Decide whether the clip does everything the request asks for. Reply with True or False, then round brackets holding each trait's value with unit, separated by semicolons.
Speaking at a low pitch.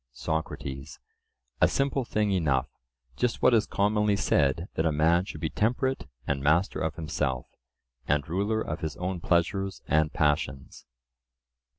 True (85 Hz)